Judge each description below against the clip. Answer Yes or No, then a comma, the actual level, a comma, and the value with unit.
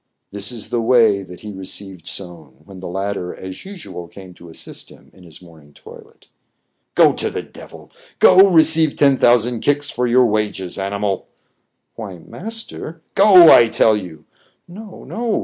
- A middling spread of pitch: No, wide, 7.8 semitones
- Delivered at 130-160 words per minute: No, average, 185 wpm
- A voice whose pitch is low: Yes, low, 105 Hz